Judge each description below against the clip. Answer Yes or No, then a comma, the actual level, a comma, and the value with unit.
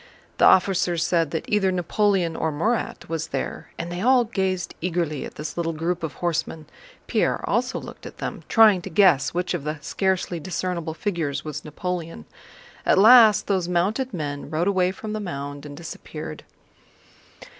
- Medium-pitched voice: Yes, medium, 175 Hz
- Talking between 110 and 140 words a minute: No, average, 165 wpm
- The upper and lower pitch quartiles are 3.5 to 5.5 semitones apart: No, average, 3.1 semitones